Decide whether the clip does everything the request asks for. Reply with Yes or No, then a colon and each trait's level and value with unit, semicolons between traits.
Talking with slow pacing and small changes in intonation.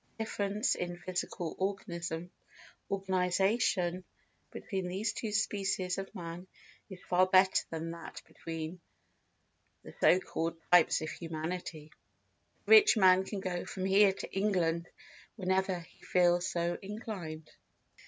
Yes: slow, 125 wpm; narrow, 2.2 semitones